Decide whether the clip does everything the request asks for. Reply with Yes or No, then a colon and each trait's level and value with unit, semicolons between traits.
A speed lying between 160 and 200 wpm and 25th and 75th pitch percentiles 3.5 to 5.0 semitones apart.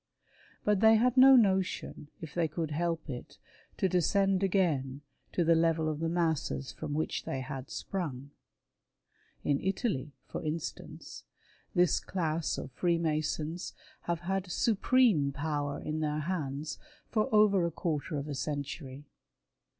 No: average, 140 wpm; average, 4.2 semitones